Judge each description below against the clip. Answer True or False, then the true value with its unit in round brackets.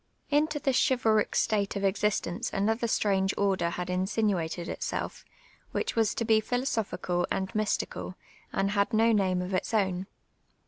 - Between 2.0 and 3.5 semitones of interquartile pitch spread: True (2.9 semitones)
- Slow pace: False (150 wpm)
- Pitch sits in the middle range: False (200 Hz)